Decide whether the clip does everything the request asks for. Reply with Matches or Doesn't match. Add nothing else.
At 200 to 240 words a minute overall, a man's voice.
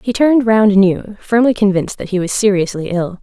Doesn't match